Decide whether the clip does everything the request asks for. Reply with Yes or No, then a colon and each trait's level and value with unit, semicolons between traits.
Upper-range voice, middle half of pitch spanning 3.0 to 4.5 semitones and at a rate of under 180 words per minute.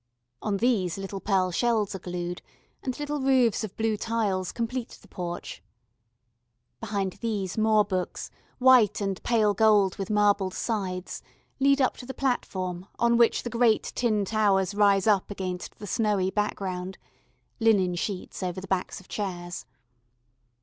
Yes: high, 205 Hz; average, 3.3 semitones; average, 150 wpm